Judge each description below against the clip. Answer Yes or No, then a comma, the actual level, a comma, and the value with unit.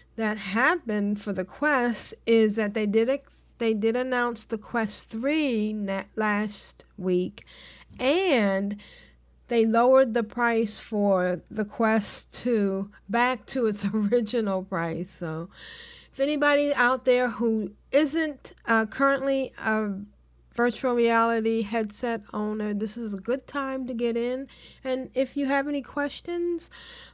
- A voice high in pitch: Yes, high, 230 Hz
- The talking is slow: Yes, slow, 130 wpm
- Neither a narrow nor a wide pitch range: Yes, average, 3.7 semitones